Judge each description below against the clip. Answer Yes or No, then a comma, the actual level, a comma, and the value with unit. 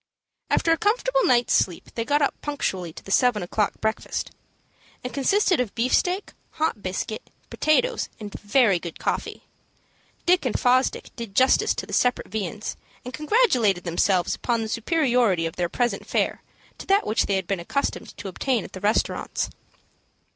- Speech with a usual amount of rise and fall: No, wide, 6.5 semitones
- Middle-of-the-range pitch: No, high, 235 Hz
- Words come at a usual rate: Yes, average, 165 wpm